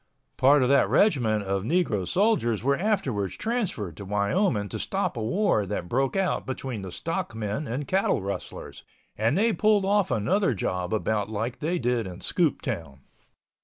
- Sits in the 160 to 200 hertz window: No, low, 125 Hz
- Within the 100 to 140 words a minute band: No, average, 165 wpm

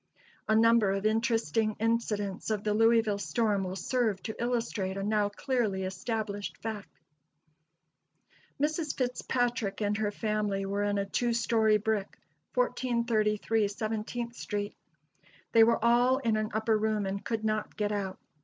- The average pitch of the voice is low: No, high, 215 Hz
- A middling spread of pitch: No, narrow, 2.2 semitones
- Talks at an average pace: Yes, average, 145 wpm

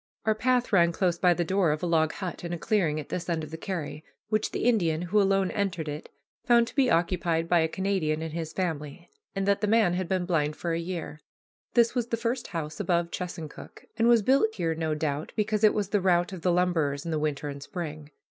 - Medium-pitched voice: Yes, medium, 175 Hz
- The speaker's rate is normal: No, fast, 240 wpm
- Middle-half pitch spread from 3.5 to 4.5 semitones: Yes, average, 3.9 semitones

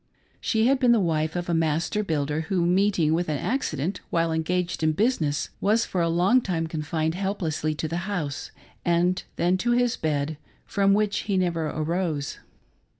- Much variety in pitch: No, average, 3.9 semitones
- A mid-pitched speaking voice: Yes, medium, 170 Hz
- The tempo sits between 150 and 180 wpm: Yes, average, 175 wpm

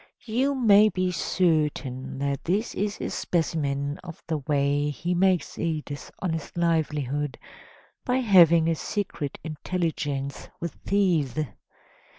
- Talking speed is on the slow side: Yes, slow, 120 wpm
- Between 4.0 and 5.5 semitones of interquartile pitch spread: Yes, average, 4.3 semitones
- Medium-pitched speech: Yes, medium, 165 Hz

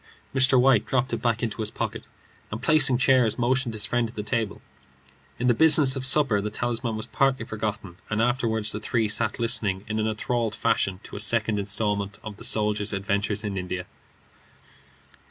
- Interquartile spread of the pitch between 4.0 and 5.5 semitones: No, average, 2.9 semitones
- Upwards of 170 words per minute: Yes, average, 185 wpm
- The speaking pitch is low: Yes, low, 110 Hz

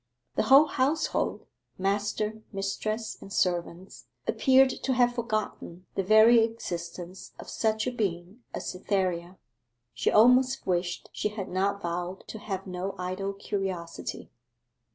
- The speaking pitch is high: Yes, high, 195 Hz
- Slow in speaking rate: Yes, slow, 130 wpm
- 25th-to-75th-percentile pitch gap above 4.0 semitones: No, average, 3.4 semitones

